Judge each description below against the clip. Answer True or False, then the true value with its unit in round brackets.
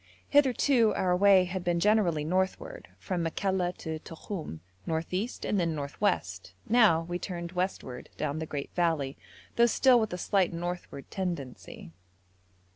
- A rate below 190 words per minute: True (150 wpm)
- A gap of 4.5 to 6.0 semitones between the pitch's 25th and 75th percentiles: False (3.8 semitones)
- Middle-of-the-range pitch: True (180 Hz)